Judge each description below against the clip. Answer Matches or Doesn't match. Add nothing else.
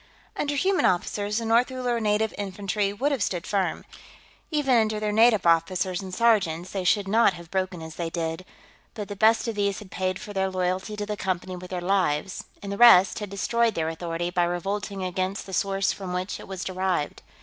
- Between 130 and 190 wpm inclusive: Doesn't match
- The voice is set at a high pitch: Matches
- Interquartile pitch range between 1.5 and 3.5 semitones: Matches